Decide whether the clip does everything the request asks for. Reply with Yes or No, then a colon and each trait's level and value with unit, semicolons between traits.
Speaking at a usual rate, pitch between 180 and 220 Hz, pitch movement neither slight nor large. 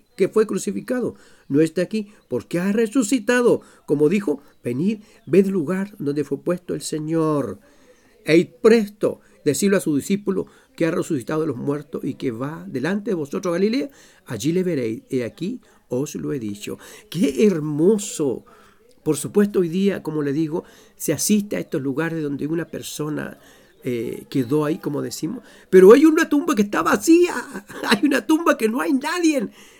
No: average, 165 wpm; medium, 185 Hz; wide, 6.9 semitones